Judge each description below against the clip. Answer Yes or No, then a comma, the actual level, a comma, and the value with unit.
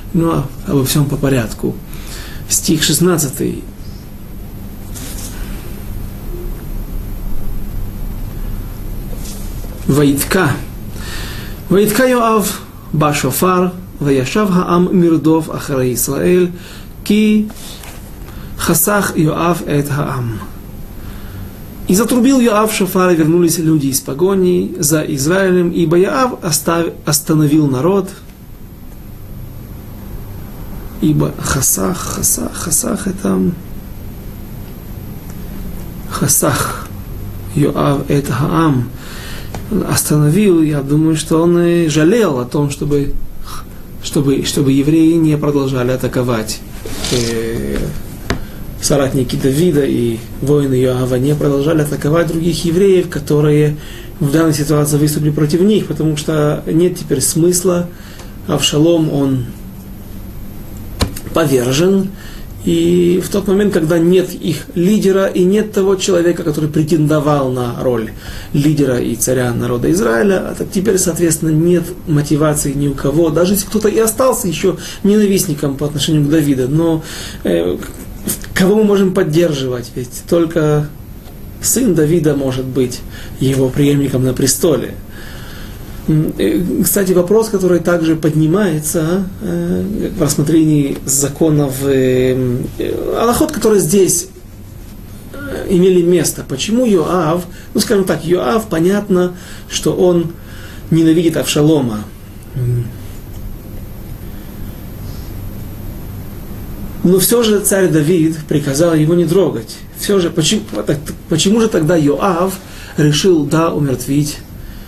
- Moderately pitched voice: Yes, medium, 150 Hz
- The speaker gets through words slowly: Yes, slow, 100 wpm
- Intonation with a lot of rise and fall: Yes, wide, 7.7 semitones